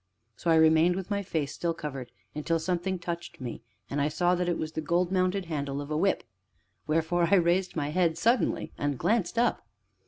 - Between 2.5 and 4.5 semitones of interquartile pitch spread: Yes, average, 2.9 semitones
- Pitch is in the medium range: Yes, medium, 170 Hz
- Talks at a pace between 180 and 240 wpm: Yes, average, 200 wpm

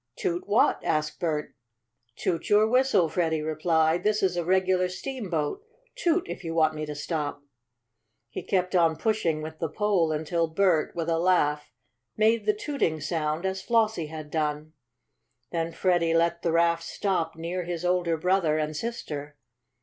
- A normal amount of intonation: Yes, average, 3.3 semitones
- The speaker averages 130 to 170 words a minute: Yes, average, 160 wpm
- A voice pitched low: No, medium, 170 Hz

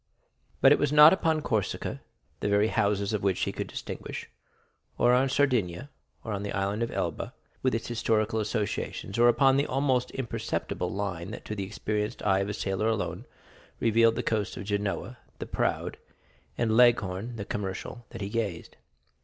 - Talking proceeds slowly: No, average, 175 wpm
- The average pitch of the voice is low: Yes, low, 110 Hz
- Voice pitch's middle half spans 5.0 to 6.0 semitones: No, average, 3.2 semitones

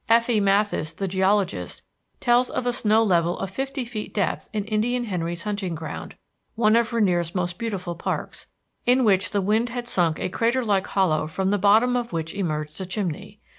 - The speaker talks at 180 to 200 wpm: Yes, average, 185 wpm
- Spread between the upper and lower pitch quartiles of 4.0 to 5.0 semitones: Yes, average, 4.6 semitones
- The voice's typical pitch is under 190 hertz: No, high, 200 Hz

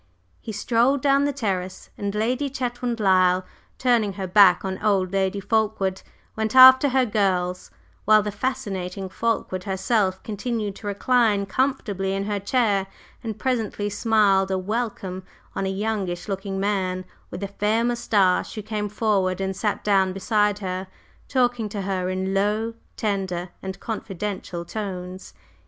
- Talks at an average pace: Yes, average, 145 wpm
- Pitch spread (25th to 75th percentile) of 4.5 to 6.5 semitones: No, average, 2.7 semitones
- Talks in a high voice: Yes, high, 205 Hz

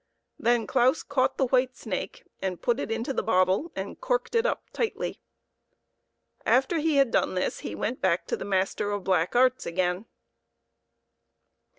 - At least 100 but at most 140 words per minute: No, average, 165 wpm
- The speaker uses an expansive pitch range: Yes, wide, 6.0 semitones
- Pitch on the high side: Yes, high, 240 Hz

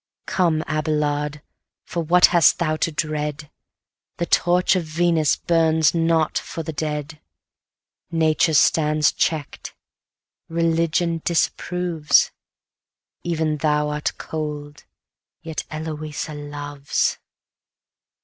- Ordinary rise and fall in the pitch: No, narrow, 1.8 semitones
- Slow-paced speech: Yes, slow, 95 wpm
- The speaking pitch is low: No, medium, 155 Hz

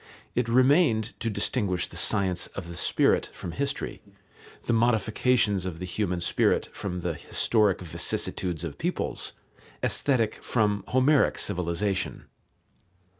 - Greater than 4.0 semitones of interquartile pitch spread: Yes, average, 4.7 semitones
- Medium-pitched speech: No, low, 100 Hz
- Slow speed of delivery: Yes, slow, 125 wpm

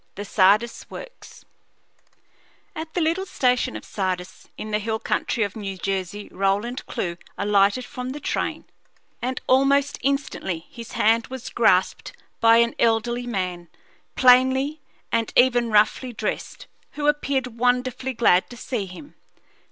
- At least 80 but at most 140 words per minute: Yes, slow, 135 wpm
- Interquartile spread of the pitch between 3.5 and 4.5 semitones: Yes, average, 4.1 semitones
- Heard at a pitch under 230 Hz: No, high, 235 Hz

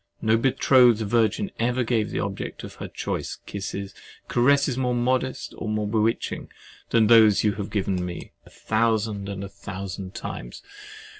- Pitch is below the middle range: Yes, low, 110 Hz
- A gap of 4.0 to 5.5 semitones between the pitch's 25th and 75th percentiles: No, average, 3.2 semitones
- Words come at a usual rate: Yes, average, 155 wpm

